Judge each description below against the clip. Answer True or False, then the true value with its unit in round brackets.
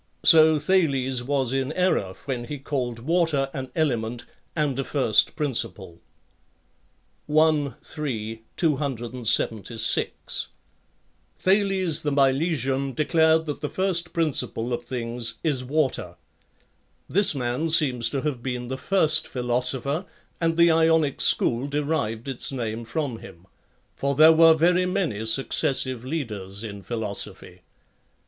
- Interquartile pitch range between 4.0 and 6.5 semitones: True (4.7 semitones)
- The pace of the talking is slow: True (120 wpm)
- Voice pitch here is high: False (135 Hz)